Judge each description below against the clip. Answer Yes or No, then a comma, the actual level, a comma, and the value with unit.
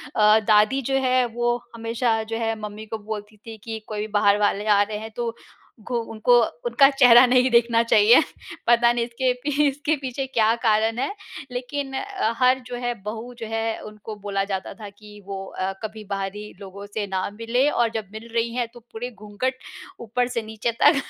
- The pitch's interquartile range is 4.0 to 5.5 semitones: No, average, 2.7 semitones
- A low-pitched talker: No, high, 225 Hz